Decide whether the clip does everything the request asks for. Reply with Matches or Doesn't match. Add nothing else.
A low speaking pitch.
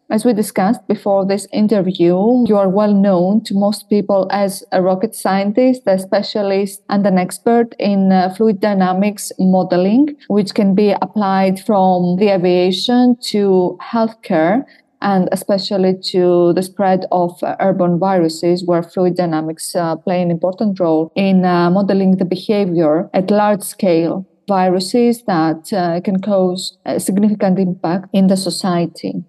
Doesn't match